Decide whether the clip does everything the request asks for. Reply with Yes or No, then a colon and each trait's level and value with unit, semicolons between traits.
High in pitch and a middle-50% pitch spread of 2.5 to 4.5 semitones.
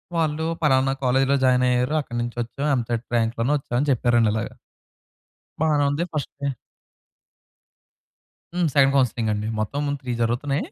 No: low, 130 Hz; average, 3.3 semitones